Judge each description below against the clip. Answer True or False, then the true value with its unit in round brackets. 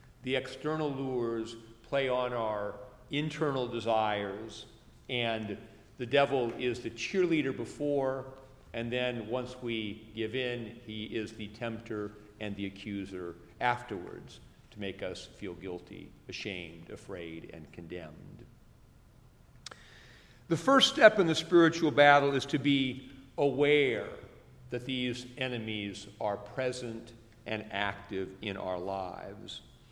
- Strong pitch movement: False (4.0 semitones)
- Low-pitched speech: True (115 Hz)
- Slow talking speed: True (120 wpm)